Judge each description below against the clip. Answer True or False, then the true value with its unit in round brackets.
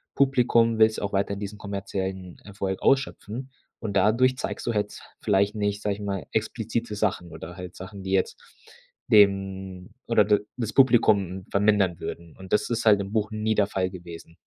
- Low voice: True (100 Hz)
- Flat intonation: True (2.3 semitones)